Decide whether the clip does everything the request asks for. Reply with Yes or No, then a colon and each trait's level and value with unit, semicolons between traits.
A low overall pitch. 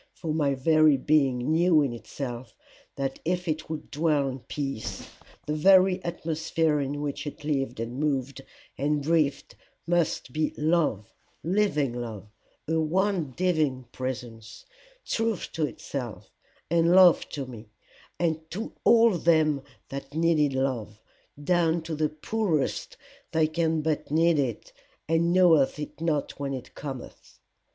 No: medium, 150 Hz